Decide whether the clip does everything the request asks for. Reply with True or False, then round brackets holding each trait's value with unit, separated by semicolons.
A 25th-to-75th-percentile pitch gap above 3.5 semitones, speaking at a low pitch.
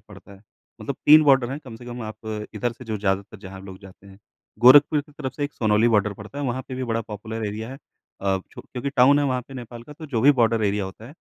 True (4.1 semitones; 115 Hz)